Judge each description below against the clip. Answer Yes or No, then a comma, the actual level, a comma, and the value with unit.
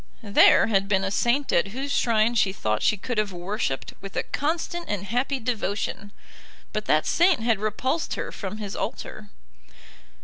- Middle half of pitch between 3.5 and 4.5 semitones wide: Yes, average, 4.0 semitones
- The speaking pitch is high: Yes, high, 215 Hz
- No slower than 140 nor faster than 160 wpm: No, average, 170 wpm